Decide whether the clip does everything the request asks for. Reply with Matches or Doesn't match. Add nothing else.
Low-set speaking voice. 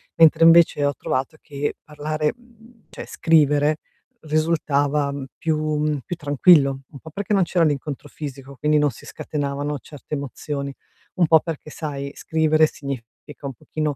Doesn't match